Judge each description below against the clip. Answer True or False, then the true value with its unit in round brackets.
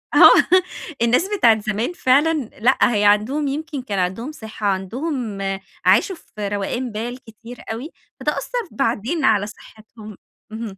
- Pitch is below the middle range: False (230 Hz)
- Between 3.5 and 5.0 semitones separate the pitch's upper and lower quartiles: True (4.6 semitones)